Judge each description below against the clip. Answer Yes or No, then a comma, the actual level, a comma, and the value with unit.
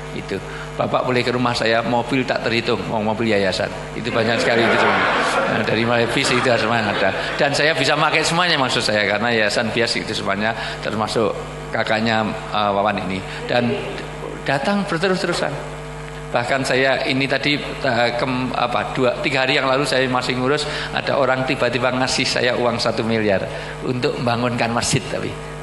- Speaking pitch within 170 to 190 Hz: No, low, 125 Hz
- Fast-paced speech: Yes, fast, 170 wpm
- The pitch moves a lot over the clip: No, average, 3.2 semitones